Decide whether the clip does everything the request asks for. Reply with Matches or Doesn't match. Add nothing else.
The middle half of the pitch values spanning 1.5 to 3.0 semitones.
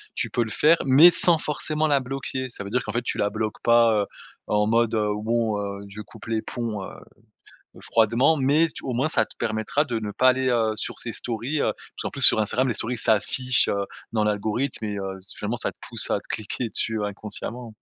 Doesn't match